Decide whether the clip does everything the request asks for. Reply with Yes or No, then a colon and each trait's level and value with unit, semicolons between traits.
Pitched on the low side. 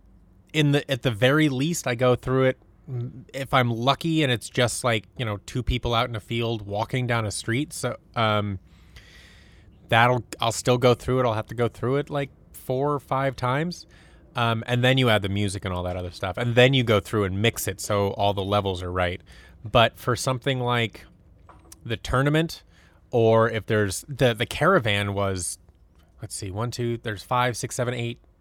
Yes: low, 115 Hz